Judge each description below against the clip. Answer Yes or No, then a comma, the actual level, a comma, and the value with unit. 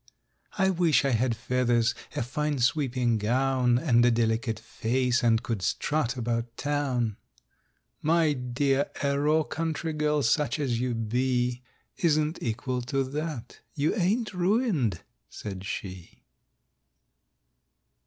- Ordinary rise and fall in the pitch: Yes, average, 4.2 semitones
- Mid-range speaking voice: No, low, 130 Hz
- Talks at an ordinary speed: No, slow, 120 wpm